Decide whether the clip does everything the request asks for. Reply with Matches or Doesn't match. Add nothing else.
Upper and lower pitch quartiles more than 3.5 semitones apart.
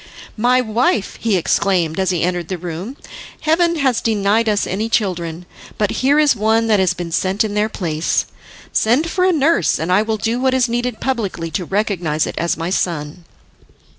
Matches